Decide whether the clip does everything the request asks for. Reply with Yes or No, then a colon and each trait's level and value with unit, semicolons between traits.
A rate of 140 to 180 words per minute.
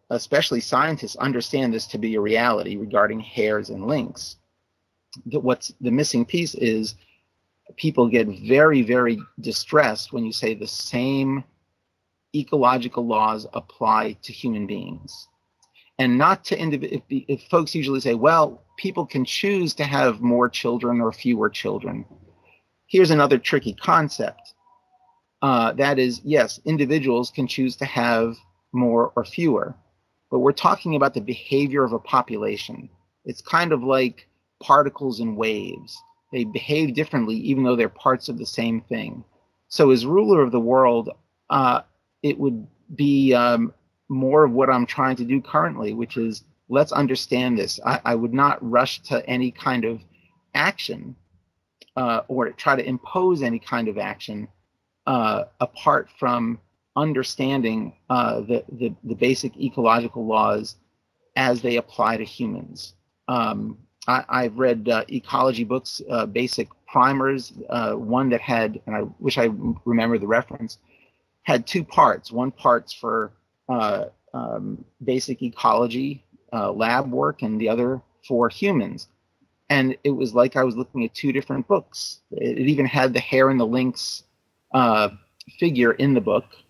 Yes: average, 150 wpm